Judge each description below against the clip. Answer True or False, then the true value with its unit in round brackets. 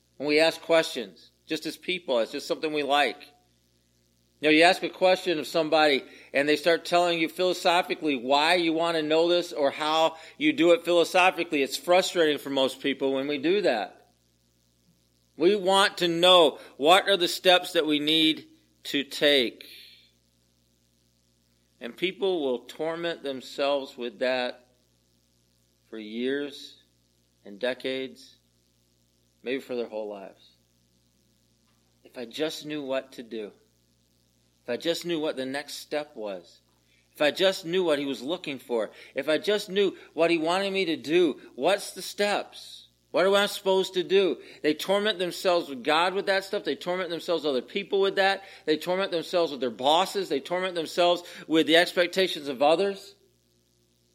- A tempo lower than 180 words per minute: True (165 wpm)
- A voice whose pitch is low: False (150 Hz)